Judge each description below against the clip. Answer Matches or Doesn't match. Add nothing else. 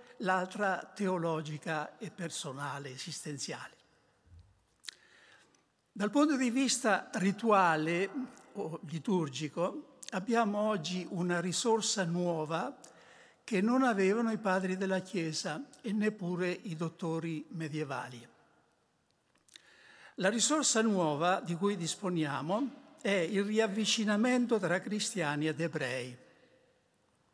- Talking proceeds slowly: Matches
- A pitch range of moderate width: Matches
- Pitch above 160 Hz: Matches